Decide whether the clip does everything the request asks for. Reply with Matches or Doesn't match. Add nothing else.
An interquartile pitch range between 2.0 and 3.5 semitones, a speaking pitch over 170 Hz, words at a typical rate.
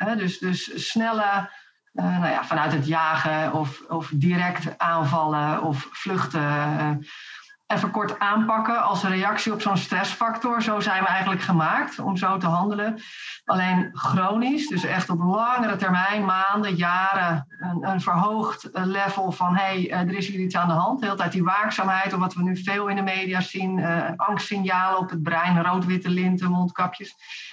Matches